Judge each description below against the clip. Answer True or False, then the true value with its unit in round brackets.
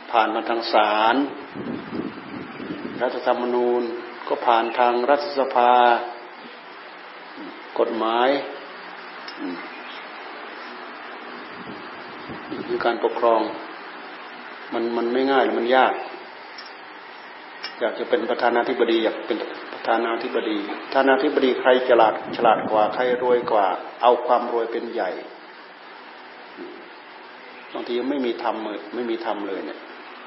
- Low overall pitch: True (120 Hz)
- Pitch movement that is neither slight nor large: False (2.1 semitones)